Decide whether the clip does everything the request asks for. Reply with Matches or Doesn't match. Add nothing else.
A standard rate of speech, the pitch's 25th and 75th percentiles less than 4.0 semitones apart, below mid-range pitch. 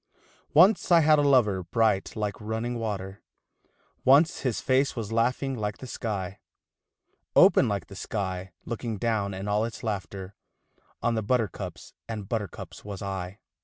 Matches